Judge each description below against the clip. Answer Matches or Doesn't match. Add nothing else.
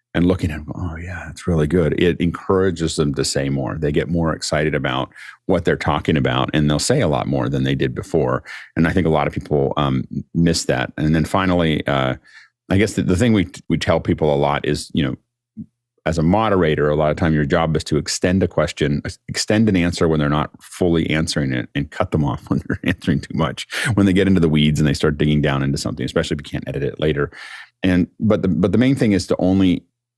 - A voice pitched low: Matches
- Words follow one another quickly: Matches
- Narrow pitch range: Doesn't match